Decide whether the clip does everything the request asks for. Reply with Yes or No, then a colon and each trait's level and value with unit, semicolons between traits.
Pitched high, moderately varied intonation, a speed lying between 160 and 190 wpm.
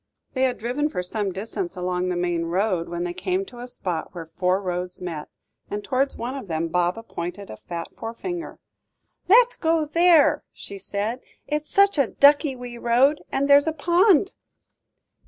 No: high, 230 Hz; wide, 8.5 semitones; average, 180 wpm